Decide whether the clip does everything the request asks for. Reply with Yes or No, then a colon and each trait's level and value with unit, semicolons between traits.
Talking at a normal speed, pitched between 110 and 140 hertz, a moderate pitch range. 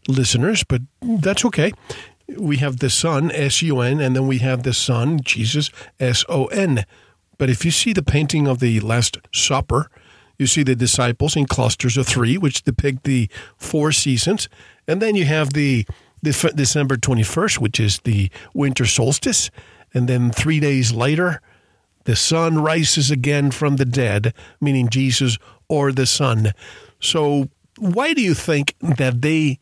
Yes: average, 165 wpm; low, 135 Hz; average, 3.4 semitones